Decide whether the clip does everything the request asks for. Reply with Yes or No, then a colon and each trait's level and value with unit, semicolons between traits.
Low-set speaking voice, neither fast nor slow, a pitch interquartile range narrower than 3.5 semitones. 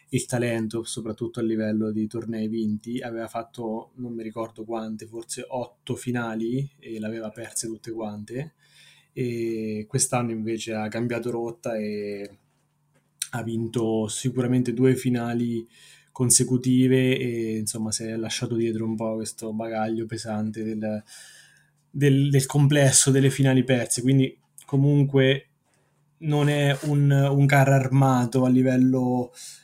Yes: low, 120 Hz; average, 130 wpm; average, 2.9 semitones